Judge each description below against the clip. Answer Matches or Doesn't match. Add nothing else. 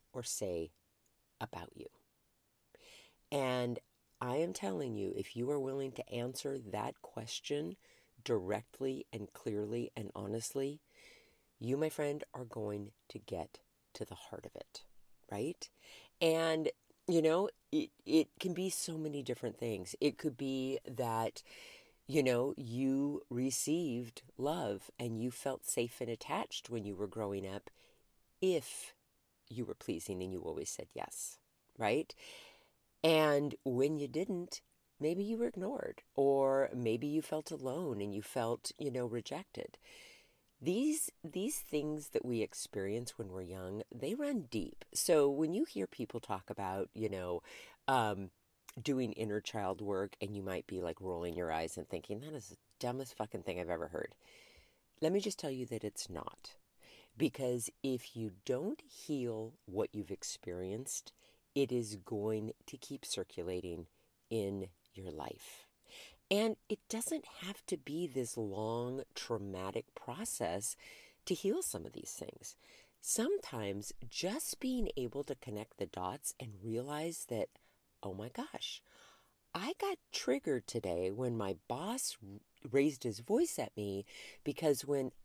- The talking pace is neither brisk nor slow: Matches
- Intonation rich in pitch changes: Matches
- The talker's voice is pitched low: Matches